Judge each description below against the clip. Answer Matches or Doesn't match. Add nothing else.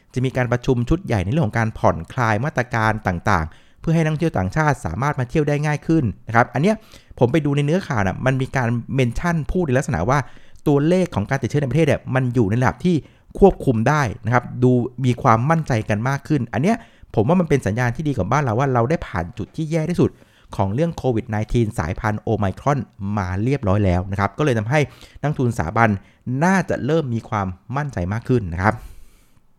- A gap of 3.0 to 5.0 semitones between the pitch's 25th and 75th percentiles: Doesn't match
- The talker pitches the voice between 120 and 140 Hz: Matches